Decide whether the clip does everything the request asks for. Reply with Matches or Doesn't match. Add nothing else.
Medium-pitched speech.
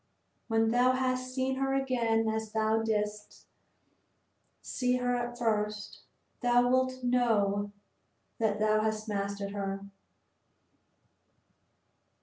Doesn't match